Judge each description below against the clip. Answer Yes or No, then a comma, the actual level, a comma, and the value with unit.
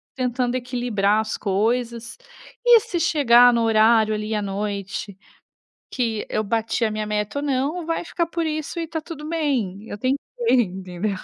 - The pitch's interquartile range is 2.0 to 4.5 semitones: No, average, 5.1 semitones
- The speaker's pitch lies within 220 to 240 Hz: Yes, high, 235 Hz